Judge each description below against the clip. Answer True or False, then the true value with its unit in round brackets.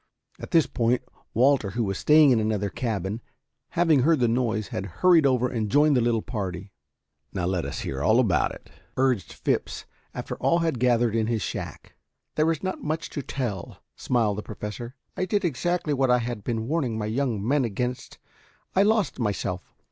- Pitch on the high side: False (120 Hz)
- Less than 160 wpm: False (185 wpm)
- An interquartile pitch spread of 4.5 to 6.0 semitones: True (5.0 semitones)